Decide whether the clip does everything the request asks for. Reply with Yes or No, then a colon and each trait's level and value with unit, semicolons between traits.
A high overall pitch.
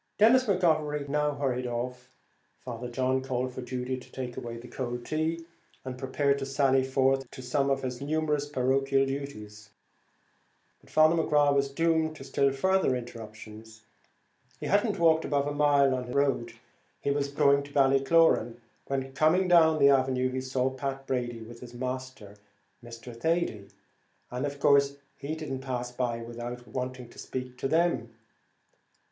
No: low, 135 Hz